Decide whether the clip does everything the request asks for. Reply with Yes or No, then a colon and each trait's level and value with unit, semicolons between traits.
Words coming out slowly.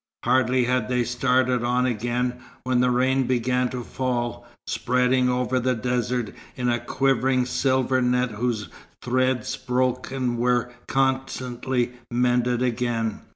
Yes: slow, 125 wpm